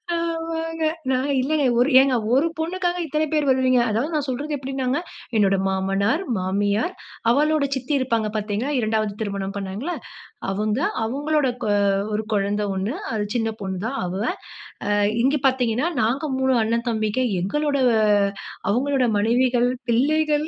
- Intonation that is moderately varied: No, wide, 5.7 semitones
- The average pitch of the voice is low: No, very high, 255 Hz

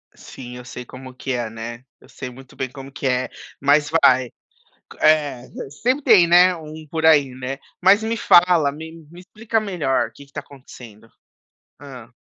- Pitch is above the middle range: No, medium, 140 Hz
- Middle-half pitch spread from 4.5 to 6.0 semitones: Yes, average, 4.9 semitones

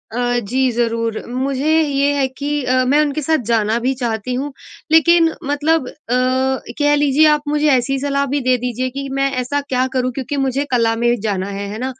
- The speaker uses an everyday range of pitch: Yes, average, 3.0 semitones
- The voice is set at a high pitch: Yes, very high, 265 Hz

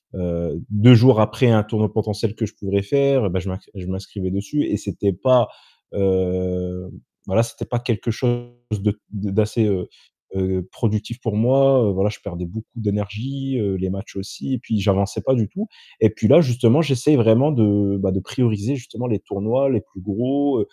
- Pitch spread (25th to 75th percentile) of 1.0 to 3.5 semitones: No, average, 3.9 semitones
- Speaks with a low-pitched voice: Yes, low, 105 Hz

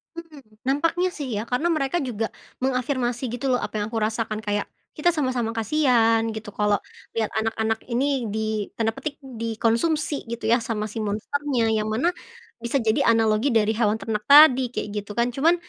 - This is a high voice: Yes, high, 235 Hz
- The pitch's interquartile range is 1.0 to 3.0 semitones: No, average, 3.7 semitones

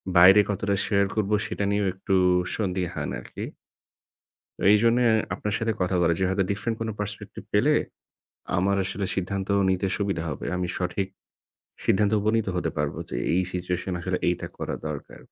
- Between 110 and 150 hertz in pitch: No, very low, 95 Hz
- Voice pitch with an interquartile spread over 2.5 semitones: No, narrow, 2.2 semitones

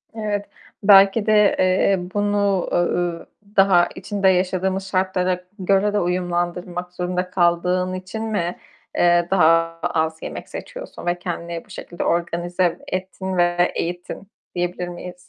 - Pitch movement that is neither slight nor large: No, narrow, 1.7 semitones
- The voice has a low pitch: No, medium, 180 Hz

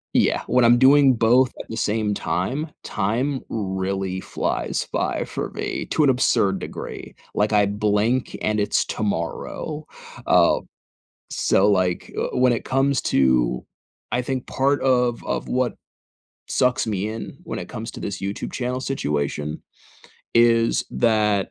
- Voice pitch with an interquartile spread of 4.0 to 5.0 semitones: Yes, average, 4.3 semitones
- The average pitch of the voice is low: Yes, low, 110 Hz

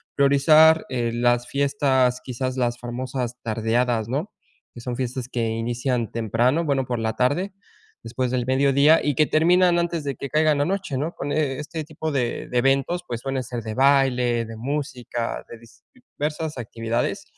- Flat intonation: No, average, 3.4 semitones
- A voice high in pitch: No, low, 130 Hz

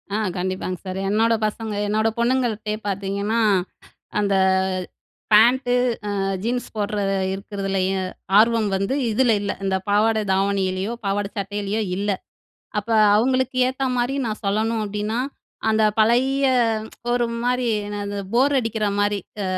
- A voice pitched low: No, high, 215 Hz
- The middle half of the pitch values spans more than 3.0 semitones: No, average, 2.7 semitones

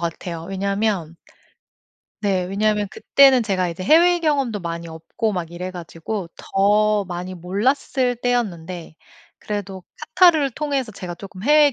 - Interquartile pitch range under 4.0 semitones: No, wide, 5.6 semitones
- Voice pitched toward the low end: No, high, 200 Hz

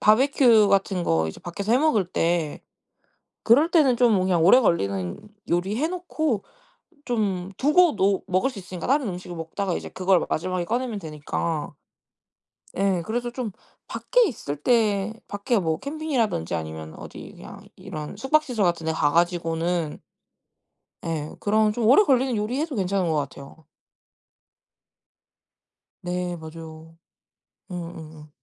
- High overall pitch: Yes, high, 195 Hz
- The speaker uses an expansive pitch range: Yes, wide, 6.6 semitones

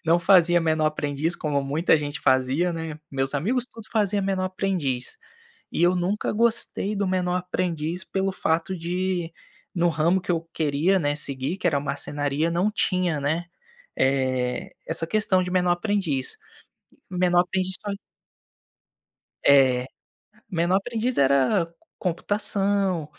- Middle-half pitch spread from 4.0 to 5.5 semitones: Yes, average, 4.3 semitones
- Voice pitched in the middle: Yes, medium, 175 Hz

